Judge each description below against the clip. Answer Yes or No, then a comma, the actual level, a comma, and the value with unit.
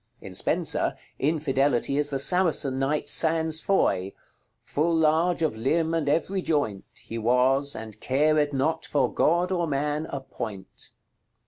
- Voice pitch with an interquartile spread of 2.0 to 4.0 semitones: Yes, average, 3.3 semitones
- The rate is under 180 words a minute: Yes, average, 140 wpm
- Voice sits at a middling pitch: Yes, medium, 150 Hz